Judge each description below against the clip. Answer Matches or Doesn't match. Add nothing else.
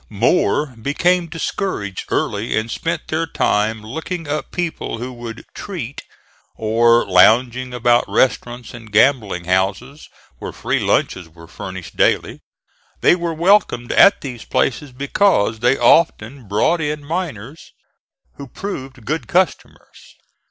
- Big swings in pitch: Matches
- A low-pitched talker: Matches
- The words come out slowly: Matches